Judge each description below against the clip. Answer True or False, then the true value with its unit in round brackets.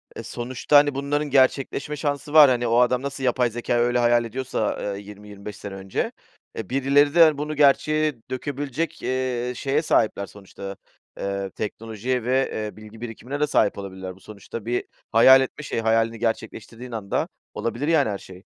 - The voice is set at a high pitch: False (120 Hz)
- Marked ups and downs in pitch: False (4.4 semitones)